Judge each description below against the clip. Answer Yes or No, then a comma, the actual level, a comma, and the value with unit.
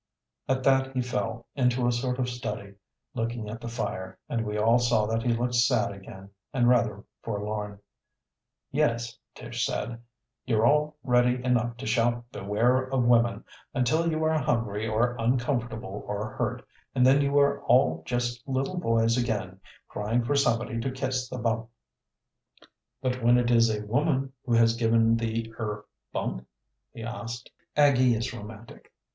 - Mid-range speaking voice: No, low, 120 Hz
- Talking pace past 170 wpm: No, average, 160 wpm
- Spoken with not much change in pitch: Yes, narrow, 2.1 semitones